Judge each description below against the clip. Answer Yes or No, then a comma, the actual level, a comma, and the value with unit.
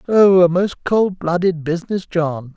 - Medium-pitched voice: Yes, medium, 175 Hz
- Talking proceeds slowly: No, average, 165 wpm